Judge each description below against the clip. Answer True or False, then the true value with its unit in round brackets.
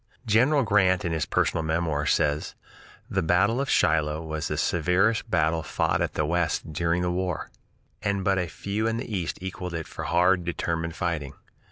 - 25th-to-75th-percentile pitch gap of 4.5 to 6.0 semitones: False (3.2 semitones)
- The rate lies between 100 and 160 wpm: False (175 wpm)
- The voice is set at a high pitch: False (85 Hz)